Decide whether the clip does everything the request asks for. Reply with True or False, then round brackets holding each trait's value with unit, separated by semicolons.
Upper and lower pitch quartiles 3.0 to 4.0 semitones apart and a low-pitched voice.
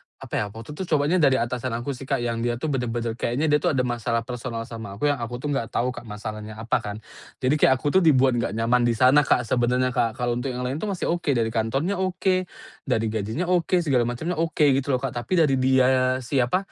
True (3.7 semitones; 125 Hz)